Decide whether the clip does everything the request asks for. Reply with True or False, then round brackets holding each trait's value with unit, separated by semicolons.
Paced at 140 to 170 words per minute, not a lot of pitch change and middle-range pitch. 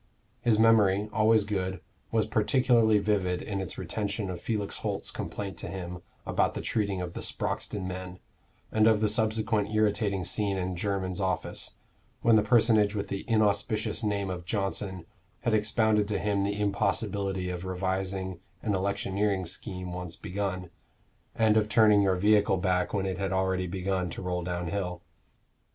False (160 wpm; 2.3 semitones; 100 Hz)